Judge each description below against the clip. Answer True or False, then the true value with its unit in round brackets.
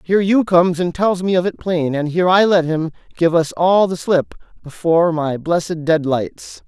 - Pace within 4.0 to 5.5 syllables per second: True (5.0 syllables/s)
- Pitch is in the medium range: True (170 Hz)